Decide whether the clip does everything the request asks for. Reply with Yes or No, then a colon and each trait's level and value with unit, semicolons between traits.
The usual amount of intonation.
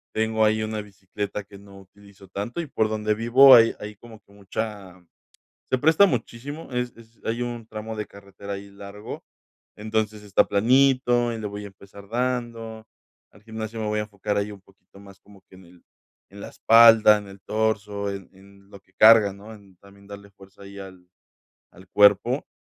No: narrow, 2.3 semitones